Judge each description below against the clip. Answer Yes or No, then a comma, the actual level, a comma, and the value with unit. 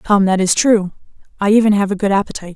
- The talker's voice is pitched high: Yes, high, 200 Hz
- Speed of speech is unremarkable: No, fast, 235 wpm